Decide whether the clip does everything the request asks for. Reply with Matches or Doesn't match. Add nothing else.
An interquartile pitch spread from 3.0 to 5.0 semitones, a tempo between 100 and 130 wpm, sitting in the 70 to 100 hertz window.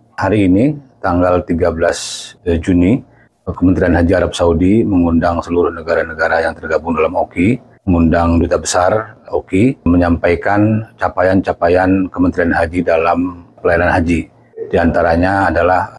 Doesn't match